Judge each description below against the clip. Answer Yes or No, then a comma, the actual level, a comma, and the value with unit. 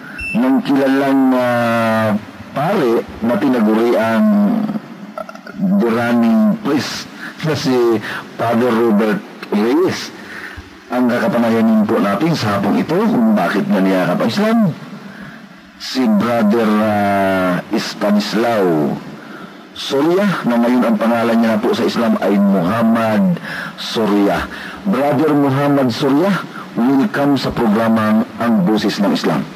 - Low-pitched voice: Yes, low, 125 Hz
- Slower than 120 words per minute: Yes, slow, 110 wpm